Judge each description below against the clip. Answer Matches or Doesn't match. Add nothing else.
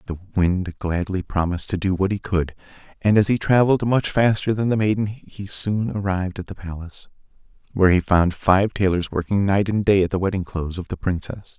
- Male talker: Matches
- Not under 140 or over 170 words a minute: Doesn't match